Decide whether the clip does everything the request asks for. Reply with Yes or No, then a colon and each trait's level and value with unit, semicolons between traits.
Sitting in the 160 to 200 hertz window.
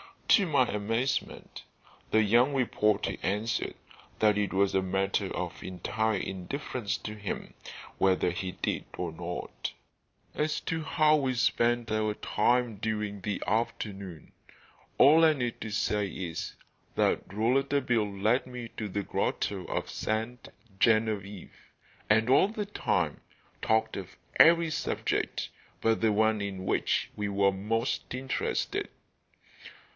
No: low, 110 Hz